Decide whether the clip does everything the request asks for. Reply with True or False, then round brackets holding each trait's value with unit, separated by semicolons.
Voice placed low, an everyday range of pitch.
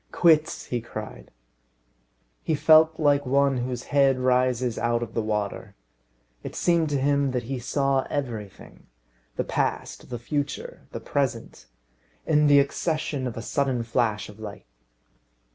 True (130 Hz; 3.4 semitones)